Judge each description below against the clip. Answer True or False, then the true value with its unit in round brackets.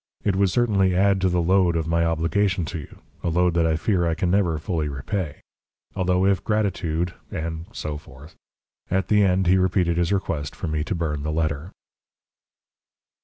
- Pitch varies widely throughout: False (2.9 semitones)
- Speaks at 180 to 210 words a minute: True (185 wpm)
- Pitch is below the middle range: True (85 Hz)